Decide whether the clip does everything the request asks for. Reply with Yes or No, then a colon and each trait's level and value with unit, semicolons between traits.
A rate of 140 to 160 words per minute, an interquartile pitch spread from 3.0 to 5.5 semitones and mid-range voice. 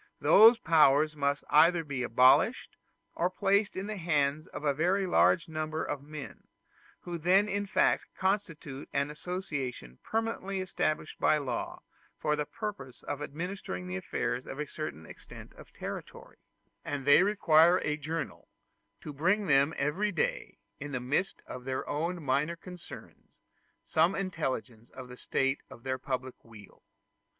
Yes: average, 150 wpm; average, 5.1 semitones; medium, 155 Hz